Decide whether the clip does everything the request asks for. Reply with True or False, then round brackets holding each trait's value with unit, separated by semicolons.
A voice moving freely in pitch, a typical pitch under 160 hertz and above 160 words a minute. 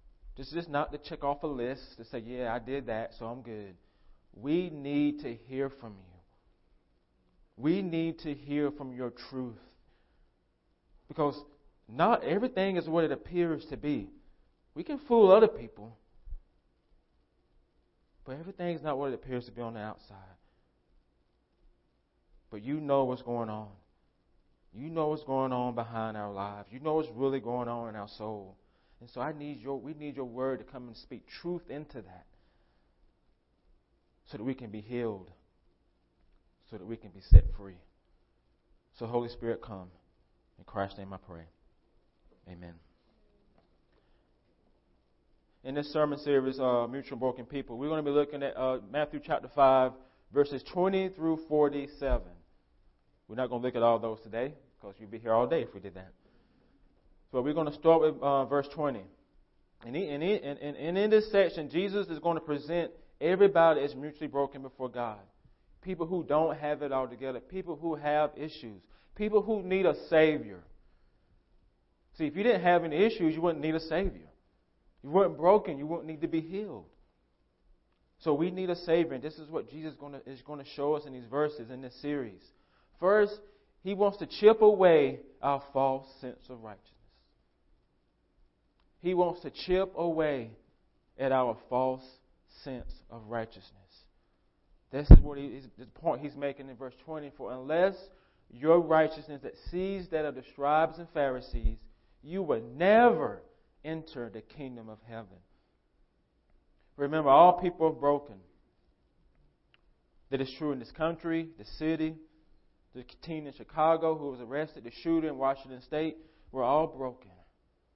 True (6.7 semitones; 135 Hz; 170 wpm)